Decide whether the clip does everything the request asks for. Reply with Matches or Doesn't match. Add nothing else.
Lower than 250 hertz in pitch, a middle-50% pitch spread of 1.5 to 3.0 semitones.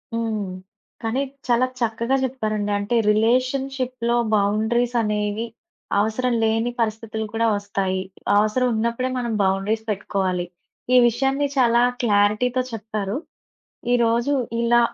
Matches